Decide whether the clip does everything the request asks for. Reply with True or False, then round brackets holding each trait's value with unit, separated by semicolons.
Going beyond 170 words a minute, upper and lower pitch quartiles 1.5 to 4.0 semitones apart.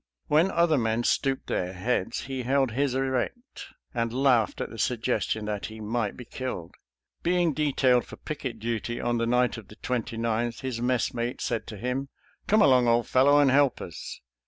True (180 wpm; 2.8 semitones)